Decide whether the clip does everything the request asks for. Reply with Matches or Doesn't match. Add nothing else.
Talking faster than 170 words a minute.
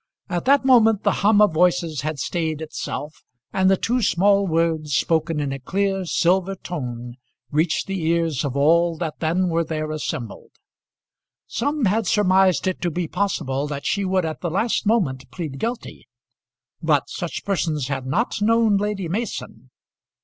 Doesn't match